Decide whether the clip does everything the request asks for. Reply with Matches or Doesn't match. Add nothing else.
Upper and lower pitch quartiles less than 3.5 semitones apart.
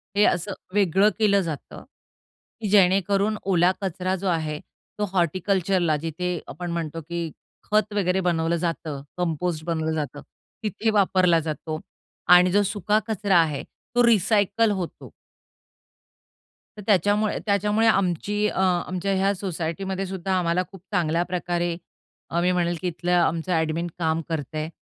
Matches